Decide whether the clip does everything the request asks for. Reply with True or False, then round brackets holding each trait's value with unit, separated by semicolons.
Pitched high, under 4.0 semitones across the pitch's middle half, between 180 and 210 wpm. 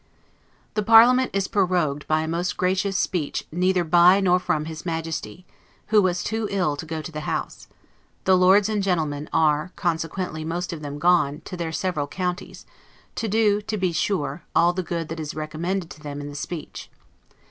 False (175 Hz; 3.4 semitones; 185 wpm)